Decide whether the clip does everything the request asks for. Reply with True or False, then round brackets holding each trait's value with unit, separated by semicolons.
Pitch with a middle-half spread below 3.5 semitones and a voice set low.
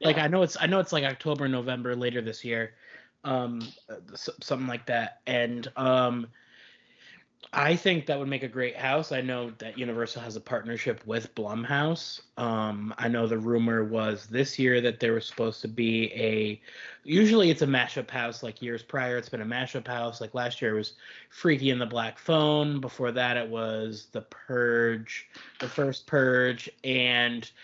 True (2.8 semitones; 125 Hz)